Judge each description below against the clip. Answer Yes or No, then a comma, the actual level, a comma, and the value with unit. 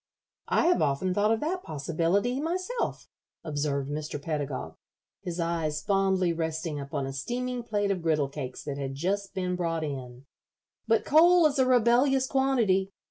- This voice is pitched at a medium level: Yes, medium, 180 Hz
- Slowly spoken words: No, average, 155 wpm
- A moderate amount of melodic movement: No, wide, 8.6 semitones